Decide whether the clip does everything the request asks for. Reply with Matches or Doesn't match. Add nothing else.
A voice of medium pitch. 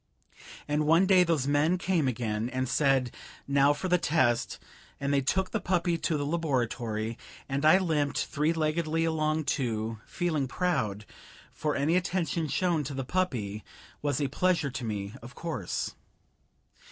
Matches